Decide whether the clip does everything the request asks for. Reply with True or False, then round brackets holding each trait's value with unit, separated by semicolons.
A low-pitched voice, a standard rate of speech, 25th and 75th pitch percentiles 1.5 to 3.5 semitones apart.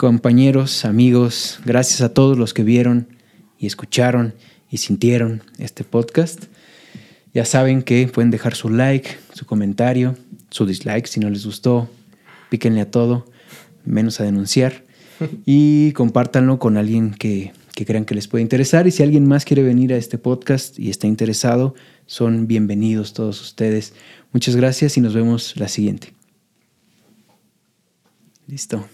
True (120 Hz; 145 wpm; 2.9 semitones)